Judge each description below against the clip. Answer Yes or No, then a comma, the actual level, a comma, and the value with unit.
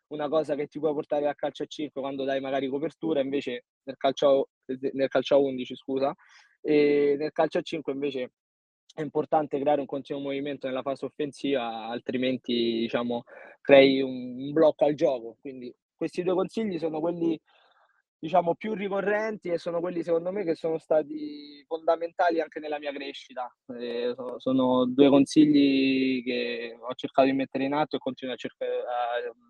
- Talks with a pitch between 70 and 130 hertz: No, medium, 140 Hz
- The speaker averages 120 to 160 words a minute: No, fast, 170 wpm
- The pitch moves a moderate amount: Yes, average, 3.1 semitones